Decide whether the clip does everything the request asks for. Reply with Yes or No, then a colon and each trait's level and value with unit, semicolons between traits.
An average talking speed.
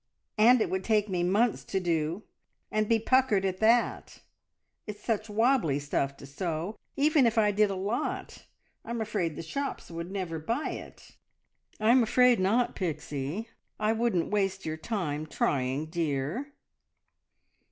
Yes: average, 150 wpm